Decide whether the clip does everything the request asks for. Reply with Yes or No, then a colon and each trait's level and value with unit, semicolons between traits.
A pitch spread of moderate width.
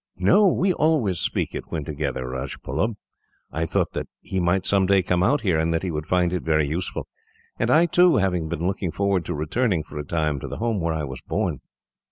Yes: average, 4.2 semitones